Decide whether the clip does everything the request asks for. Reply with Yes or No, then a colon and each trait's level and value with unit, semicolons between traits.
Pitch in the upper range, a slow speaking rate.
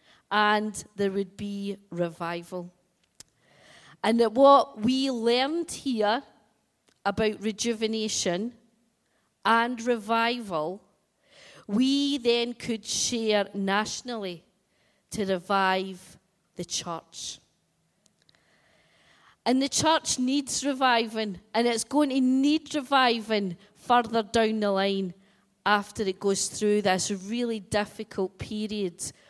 Yes: high, 215 Hz; slow, 95 wpm